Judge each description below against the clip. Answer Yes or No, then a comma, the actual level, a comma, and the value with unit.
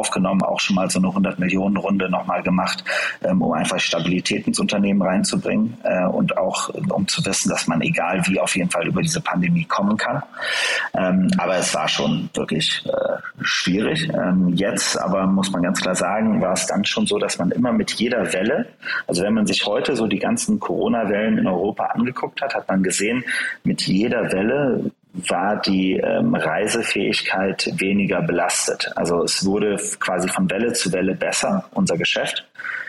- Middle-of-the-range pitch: No, low, 100 Hz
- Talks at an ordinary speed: Yes, average, 170 wpm